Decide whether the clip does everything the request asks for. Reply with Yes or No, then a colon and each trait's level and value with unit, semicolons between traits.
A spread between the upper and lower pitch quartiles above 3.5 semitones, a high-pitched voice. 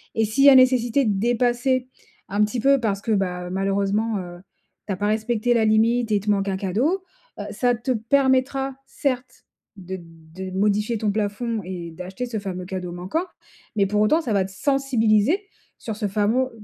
Yes: average, 4.0 semitones; high, 215 Hz